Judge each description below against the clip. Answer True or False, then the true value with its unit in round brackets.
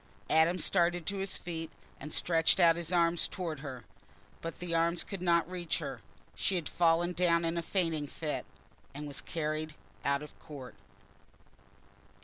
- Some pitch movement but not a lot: False (2.0 semitones)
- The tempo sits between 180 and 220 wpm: False (160 wpm)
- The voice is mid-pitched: True (165 Hz)